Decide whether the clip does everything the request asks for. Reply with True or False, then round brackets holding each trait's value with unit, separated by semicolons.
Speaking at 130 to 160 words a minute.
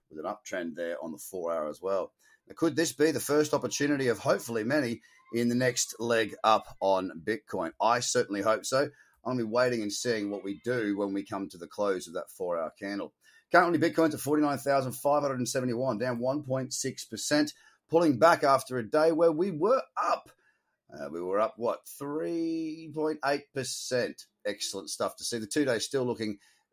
False (180 wpm)